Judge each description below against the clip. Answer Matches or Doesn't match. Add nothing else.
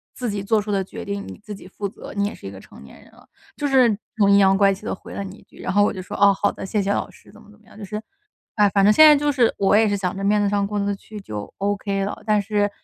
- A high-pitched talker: Matches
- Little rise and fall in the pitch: Matches